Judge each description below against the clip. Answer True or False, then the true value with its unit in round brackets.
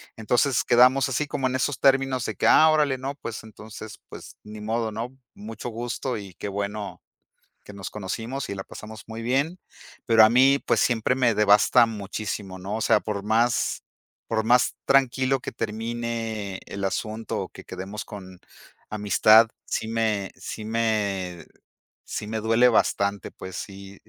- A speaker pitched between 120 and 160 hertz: False (110 Hz)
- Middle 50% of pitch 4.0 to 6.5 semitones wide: False (3.0 semitones)